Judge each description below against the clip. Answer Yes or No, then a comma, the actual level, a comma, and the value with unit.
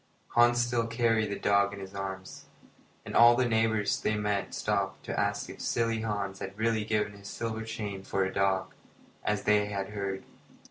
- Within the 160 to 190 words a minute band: Yes, average, 185 wpm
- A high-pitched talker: No, low, 105 Hz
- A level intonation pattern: Yes, narrow, 2.3 semitones